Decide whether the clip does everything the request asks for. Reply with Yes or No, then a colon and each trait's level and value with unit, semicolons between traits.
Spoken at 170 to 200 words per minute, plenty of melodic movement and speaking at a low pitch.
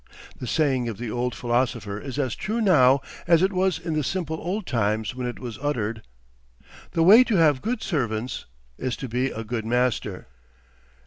Yes: average, 185 wpm; wide, 5.8 semitones; low, 130 Hz